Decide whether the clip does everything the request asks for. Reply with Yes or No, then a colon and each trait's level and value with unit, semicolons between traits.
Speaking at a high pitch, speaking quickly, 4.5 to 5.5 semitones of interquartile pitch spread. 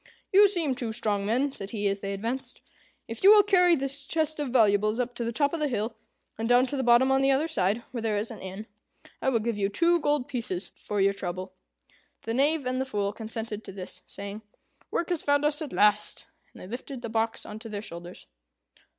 Yes: high, 235 Hz; fast, 230 wpm; average, 5.2 semitones